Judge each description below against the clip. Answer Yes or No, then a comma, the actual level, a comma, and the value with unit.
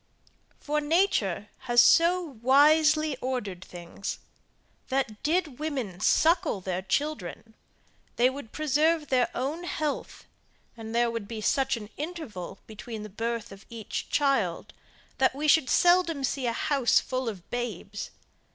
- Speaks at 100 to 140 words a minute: Yes, slow, 135 wpm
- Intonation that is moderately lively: No, wide, 5.8 semitones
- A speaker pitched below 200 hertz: No, very high, 255 Hz